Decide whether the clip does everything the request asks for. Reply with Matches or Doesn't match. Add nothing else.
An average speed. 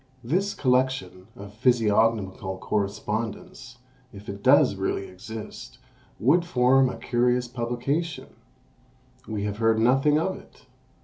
Doesn't match